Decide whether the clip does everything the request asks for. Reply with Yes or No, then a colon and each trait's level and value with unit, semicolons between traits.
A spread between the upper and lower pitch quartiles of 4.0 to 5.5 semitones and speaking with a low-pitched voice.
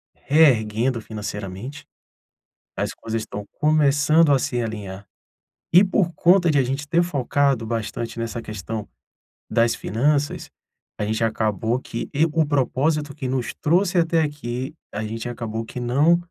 Yes: average, 5.2 semitones; low, 130 Hz